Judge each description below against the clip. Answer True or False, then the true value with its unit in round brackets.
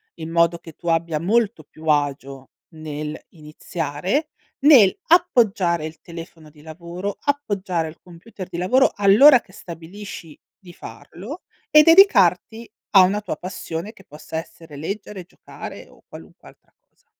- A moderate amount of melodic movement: True (4.6 semitones)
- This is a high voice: False (175 Hz)